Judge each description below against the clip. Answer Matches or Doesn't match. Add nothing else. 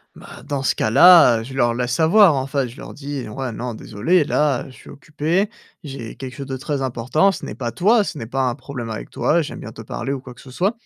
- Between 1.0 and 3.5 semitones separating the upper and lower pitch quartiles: Doesn't match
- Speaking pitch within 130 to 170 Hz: Matches